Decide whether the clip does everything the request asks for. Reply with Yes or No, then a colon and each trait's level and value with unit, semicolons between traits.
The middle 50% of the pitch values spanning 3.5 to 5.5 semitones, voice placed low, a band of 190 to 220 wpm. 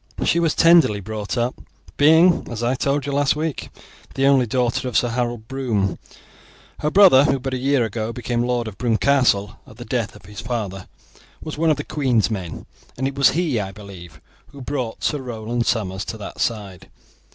Yes: average, 4.4 semitones; low, 120 Hz; average, 195 wpm